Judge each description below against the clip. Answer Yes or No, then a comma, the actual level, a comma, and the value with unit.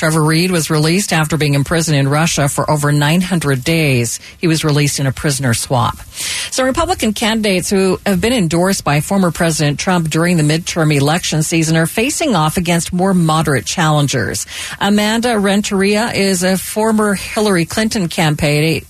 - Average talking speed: Yes, average, 160 wpm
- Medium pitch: Yes, medium, 165 Hz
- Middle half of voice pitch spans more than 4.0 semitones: Yes, average, 4.5 semitones